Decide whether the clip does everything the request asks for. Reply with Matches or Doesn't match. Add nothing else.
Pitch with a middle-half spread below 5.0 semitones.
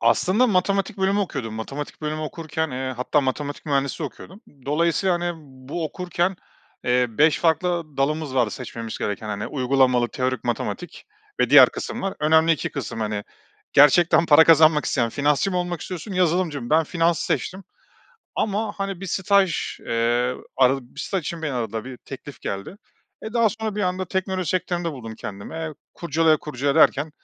Doesn't match